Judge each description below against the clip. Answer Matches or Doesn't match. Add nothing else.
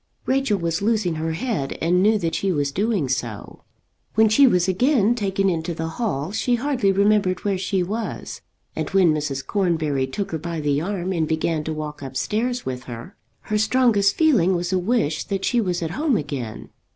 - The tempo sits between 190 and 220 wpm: Matches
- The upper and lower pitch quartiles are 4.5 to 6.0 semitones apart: Matches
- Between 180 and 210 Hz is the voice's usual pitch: Matches